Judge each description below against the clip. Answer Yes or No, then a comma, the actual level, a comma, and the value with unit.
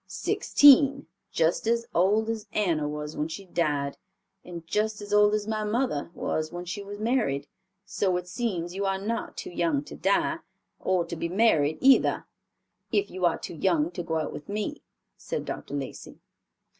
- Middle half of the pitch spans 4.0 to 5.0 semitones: Yes, average, 4.7 semitones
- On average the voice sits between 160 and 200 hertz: Yes, medium, 185 Hz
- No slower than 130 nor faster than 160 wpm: No, average, 180 wpm